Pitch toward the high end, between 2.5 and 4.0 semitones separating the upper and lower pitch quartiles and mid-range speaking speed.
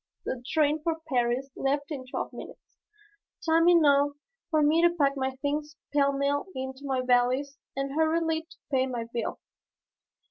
Yes: very high, 280 Hz; average, 3.0 semitones; average, 155 wpm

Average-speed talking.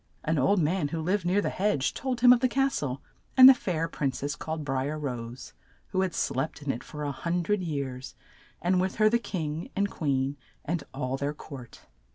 No: fast, 215 wpm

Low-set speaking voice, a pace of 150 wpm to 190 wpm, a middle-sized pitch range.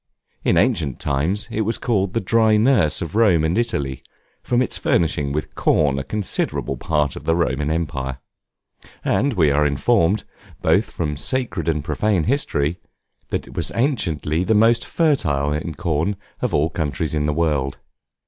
No: very low, 80 Hz; average, 165 wpm; wide, 6.6 semitones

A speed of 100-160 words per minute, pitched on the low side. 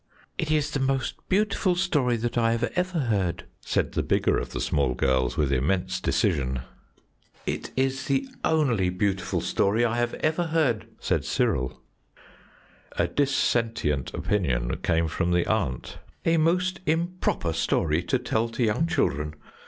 Yes: average, 145 wpm; low, 115 Hz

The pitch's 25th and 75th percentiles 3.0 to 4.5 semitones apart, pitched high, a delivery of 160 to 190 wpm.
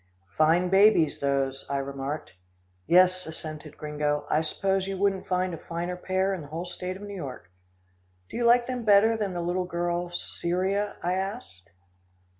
No: average, 3.7 semitones; medium, 180 Hz; average, 170 wpm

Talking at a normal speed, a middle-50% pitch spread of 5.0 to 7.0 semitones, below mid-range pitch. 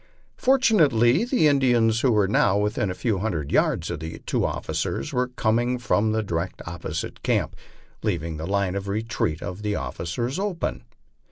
Yes: average, 170 wpm; wide, 5.6 semitones; low, 105 Hz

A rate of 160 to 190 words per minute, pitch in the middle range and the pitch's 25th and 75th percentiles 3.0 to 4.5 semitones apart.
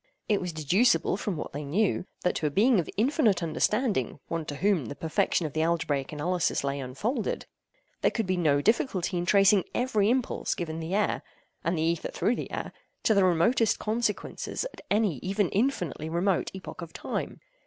No: average, 175 wpm; medium, 180 Hz; average, 4.9 semitones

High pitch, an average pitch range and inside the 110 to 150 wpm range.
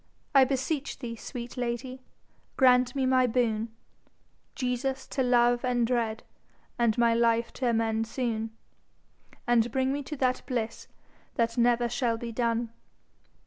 No: high, 240 Hz; narrow, 1.9 semitones; average, 140 wpm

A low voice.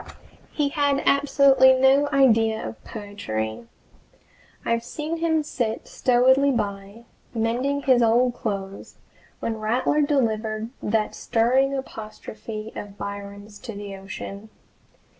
No: high, 230 Hz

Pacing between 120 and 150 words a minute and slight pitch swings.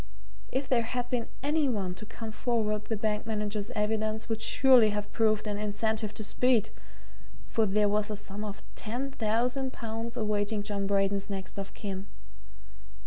No: average, 165 wpm; narrow, 1.9 semitones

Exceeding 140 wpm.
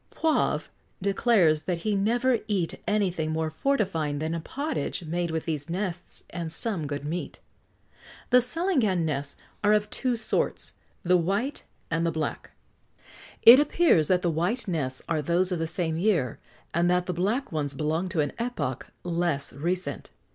Yes: average, 160 wpm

